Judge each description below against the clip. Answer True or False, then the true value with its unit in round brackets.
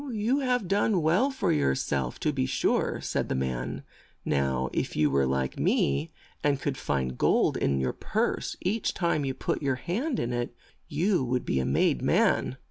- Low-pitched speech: True (125 Hz)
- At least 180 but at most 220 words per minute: True (190 wpm)